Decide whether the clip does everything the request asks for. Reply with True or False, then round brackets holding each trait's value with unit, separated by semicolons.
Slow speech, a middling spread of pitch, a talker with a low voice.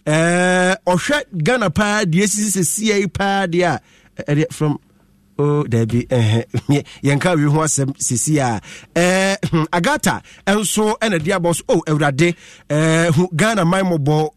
False (130 wpm; 4.6 semitones; 170 Hz)